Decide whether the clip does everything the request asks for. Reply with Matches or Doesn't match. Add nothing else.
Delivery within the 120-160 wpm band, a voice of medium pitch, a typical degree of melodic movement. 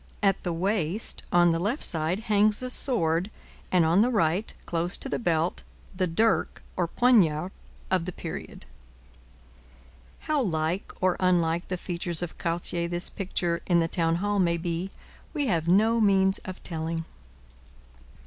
Matches